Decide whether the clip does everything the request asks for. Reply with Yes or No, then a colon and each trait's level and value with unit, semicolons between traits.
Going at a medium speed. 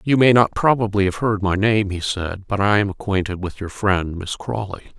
No: fast, 230 wpm